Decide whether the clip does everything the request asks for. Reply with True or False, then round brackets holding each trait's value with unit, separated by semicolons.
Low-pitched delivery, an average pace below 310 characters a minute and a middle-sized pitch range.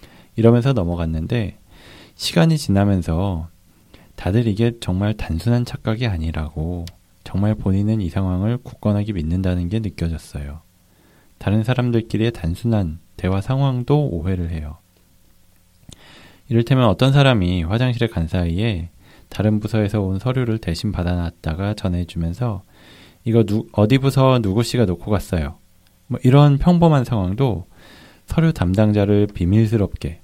True (100 Hz; 300 characters per minute; 4.7 semitones)